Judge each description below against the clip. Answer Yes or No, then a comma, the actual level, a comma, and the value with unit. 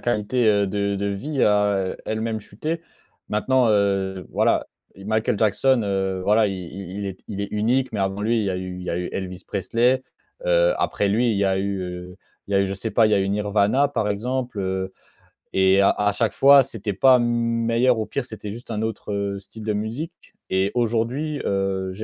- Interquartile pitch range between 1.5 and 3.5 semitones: Yes, average, 3.1 semitones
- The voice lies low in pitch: Yes, low, 105 Hz